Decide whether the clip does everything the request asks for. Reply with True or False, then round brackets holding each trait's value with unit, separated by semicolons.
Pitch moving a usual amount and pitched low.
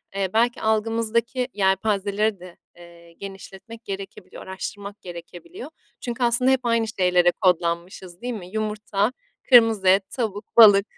False (3.5 semitones; 200 Hz)